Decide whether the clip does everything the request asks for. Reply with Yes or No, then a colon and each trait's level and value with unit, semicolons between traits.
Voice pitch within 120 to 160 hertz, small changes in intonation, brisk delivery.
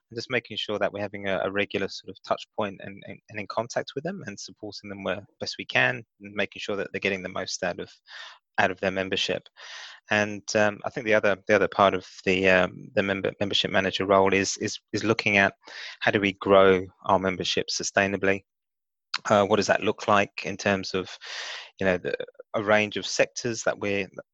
No: low, 100 Hz; narrow, 1.6 semitones; fast, 220 wpm